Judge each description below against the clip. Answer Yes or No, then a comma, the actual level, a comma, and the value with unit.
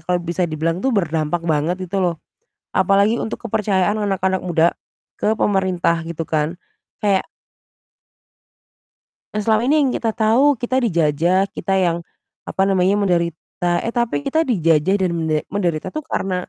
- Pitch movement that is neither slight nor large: Yes, average, 3.9 semitones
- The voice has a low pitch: No, high, 190 Hz